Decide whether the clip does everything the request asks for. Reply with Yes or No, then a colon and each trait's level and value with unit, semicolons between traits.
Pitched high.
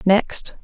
Yes: high, 200 Hz